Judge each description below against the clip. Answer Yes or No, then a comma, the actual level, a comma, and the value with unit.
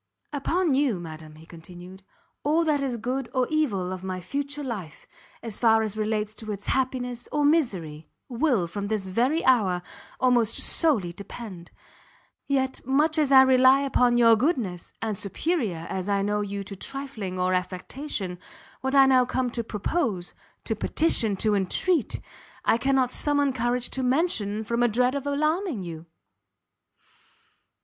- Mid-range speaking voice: No, high, 235 Hz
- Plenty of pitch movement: Yes, wide, 5.8 semitones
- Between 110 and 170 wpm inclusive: Yes, average, 155 wpm